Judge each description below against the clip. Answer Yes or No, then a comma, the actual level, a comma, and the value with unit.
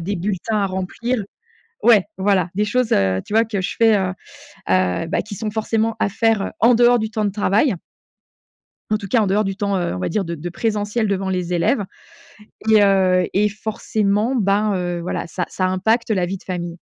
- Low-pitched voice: No, high, 200 Hz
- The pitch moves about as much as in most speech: Yes, average, 3.1 semitones